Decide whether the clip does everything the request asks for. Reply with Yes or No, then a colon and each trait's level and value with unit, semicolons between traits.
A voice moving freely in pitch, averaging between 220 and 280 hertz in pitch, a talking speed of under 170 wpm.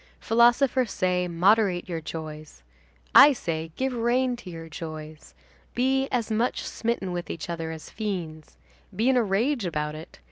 No: wide, 6.7 semitones; medium, 185 Hz; average, 155 wpm